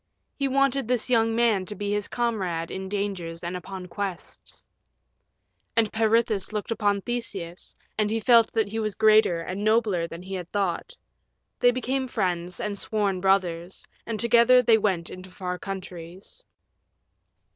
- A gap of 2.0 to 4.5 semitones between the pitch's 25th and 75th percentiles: Yes, average, 3.7 semitones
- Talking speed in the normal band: Yes, average, 155 wpm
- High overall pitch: Yes, high, 205 Hz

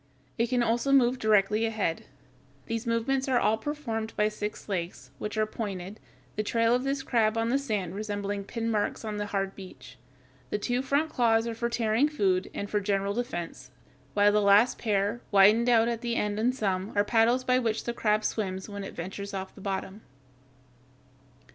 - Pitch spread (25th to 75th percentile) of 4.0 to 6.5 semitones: No, average, 2.8 semitones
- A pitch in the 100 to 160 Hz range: No, high, 215 Hz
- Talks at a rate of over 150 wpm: Yes, average, 190 wpm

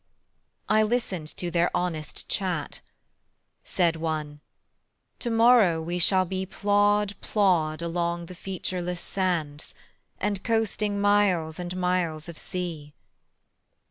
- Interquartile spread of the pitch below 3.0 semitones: No, average, 3.5 semitones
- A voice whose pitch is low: No, medium, 180 Hz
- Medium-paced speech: No, slow, 110 wpm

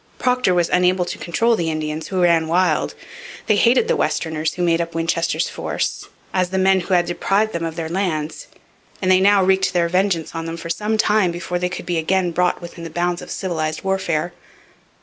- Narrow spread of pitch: Yes, narrow, 2.3 semitones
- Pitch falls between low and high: Yes, medium, 175 Hz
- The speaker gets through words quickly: Yes, fast, 210 wpm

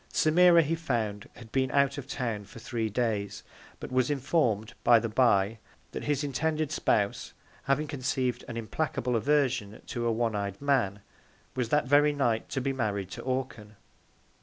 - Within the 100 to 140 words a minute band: No, average, 165 wpm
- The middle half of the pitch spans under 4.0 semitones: No, average, 4.4 semitones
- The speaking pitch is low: Yes, low, 125 Hz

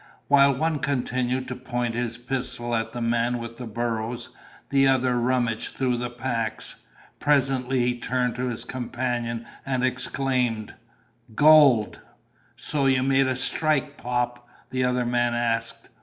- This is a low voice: Yes, low, 125 Hz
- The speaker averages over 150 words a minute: No, average, 140 wpm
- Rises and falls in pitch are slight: Yes, narrow, 1.7 semitones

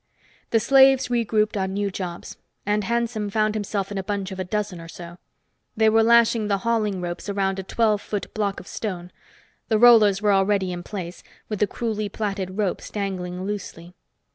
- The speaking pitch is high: Yes, high, 205 Hz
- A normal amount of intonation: No, narrow, 2.3 semitones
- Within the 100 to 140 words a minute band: No, average, 185 wpm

